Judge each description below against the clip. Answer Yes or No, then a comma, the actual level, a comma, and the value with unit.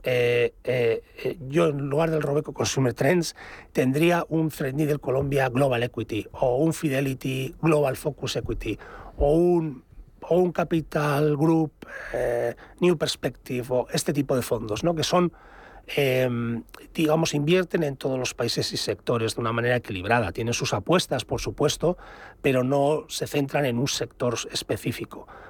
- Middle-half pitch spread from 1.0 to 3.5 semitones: No, average, 4.3 semitones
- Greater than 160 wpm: No, average, 150 wpm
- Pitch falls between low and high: Yes, medium, 145 Hz